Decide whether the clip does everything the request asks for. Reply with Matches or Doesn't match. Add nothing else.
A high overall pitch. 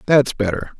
Doesn't match